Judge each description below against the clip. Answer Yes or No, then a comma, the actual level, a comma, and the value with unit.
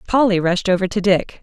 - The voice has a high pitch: Yes, high, 195 Hz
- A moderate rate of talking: No, fast, 210 wpm